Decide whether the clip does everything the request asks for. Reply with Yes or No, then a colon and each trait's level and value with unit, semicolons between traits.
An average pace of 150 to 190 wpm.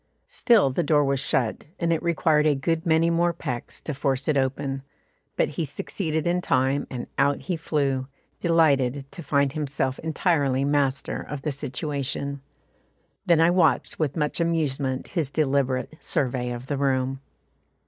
Yes: average, 160 wpm